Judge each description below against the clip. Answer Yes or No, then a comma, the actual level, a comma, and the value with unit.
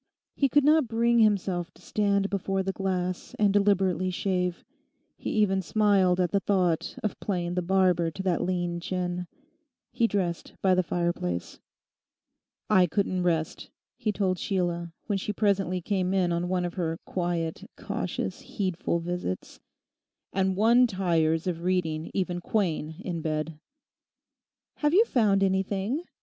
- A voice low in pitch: No, medium, 185 Hz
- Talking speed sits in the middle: Yes, average, 145 wpm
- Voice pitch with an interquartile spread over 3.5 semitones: No, narrow, 2.4 semitones